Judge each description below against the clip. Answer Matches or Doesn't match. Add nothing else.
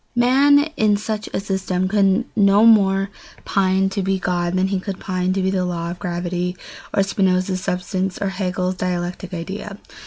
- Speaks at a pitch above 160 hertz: Matches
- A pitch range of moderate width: Doesn't match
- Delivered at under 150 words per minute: Doesn't match